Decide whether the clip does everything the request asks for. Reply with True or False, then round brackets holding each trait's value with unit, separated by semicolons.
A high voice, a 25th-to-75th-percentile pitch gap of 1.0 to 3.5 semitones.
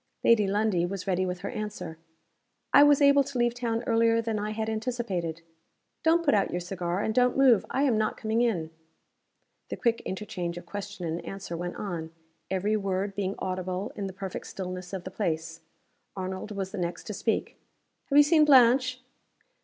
False (205 Hz; 4.1 semitones)